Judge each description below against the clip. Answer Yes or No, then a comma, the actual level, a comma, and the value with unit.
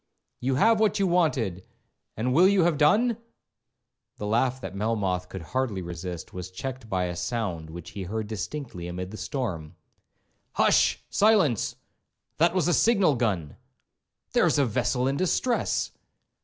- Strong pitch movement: Yes, wide, 8.9 semitones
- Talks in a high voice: No, low, 115 Hz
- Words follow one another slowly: No, average, 145 wpm